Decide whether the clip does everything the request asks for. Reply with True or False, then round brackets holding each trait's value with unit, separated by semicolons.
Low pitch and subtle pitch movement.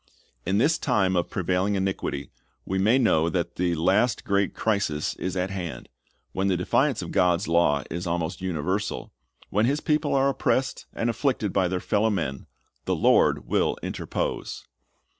False (95 Hz; 3.8 semitones)